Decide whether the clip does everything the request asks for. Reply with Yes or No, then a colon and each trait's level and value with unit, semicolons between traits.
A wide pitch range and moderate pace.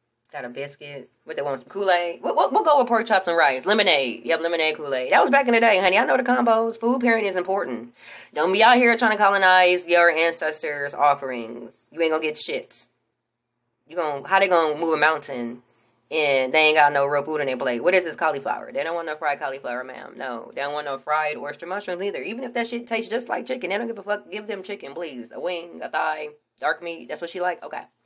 No: wide, 6.3 semitones; fast, 250 wpm